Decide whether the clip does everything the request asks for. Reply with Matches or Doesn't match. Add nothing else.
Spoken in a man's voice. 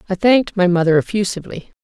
Doesn't match